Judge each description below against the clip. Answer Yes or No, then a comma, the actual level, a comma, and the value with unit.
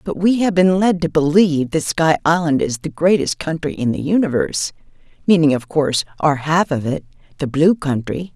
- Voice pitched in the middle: Yes, medium, 160 Hz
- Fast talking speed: No, average, 185 wpm